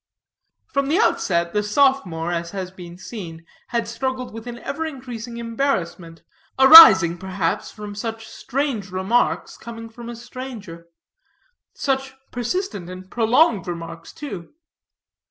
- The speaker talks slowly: Yes, slow, 125 wpm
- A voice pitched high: Yes, high, 225 Hz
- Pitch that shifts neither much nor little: No, wide, 6.1 semitones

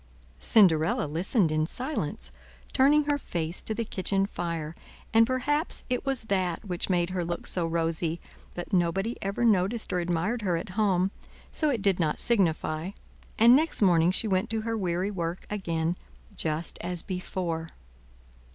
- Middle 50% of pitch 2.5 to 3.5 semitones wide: No, average, 4.8 semitones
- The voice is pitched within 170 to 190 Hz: Yes, medium, 185 Hz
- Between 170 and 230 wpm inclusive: No, average, 160 wpm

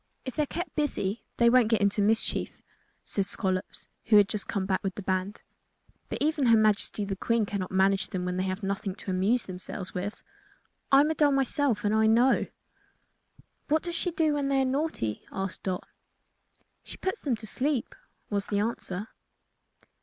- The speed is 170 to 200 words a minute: Yes, average, 185 wpm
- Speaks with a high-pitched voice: Yes, high, 215 Hz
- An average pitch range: No, wide, 5.7 semitones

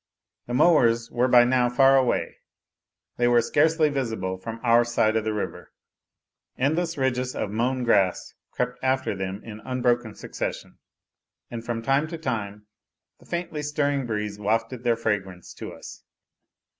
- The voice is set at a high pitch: No, low, 120 Hz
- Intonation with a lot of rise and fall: No, average, 3.2 semitones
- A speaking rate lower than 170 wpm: Yes, average, 150 wpm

